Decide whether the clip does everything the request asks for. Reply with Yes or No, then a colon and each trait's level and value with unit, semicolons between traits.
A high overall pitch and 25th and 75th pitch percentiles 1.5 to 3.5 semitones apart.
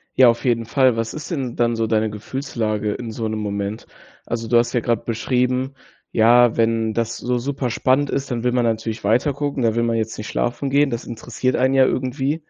No: low, 120 Hz; narrow, 2.5 semitones